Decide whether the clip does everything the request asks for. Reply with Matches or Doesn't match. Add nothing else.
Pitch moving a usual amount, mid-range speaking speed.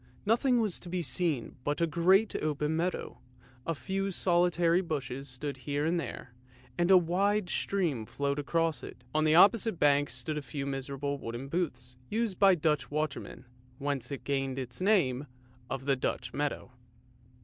Matches